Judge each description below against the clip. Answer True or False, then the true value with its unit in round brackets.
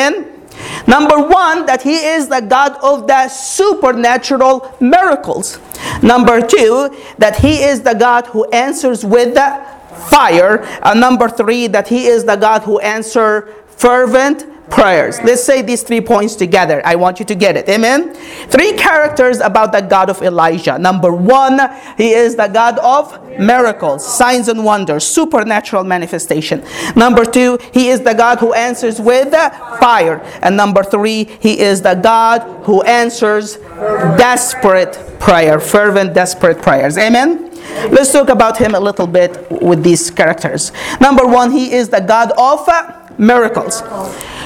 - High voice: True (235 Hz)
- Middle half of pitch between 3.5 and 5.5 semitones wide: True (4.2 semitones)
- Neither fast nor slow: True (155 wpm)